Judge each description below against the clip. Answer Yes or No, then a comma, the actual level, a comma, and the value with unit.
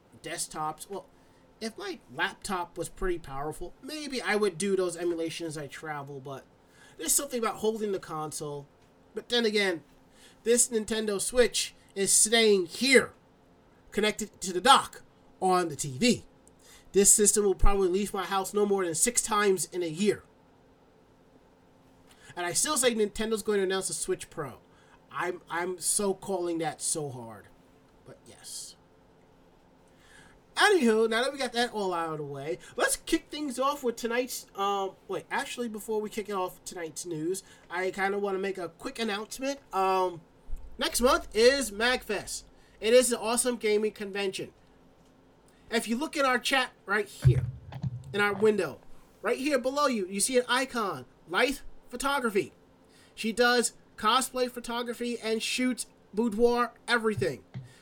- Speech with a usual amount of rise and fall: No, wide, 7.5 semitones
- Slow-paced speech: No, average, 155 wpm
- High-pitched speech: Yes, high, 195 Hz